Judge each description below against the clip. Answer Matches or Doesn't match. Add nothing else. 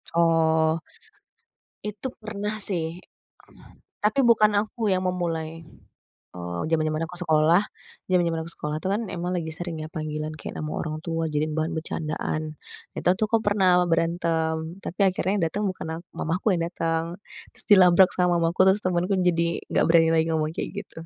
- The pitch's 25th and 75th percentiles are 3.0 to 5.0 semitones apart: Doesn't match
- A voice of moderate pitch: Matches